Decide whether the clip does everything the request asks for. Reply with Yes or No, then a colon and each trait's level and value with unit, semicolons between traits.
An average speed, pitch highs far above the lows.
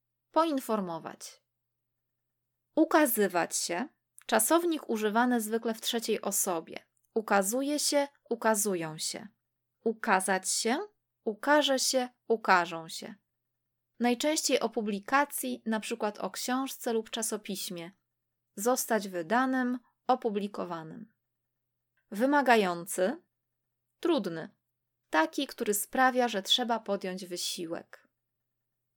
No: slow, 85 wpm; wide, 7.4 semitones